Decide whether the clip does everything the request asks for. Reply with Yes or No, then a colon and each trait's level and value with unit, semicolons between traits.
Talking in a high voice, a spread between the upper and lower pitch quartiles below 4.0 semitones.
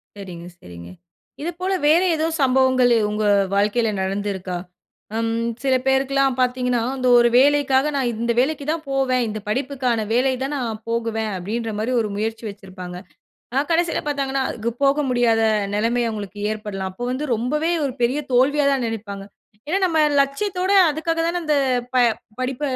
No: very high, 250 Hz; average, 4.3 semitones